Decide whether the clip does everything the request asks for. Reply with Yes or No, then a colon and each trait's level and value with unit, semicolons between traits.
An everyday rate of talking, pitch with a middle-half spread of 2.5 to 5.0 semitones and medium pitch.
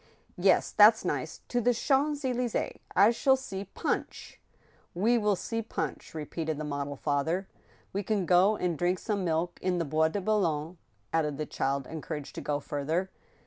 No: average, 180 wpm; wide, 5.4 semitones; medium, 180 Hz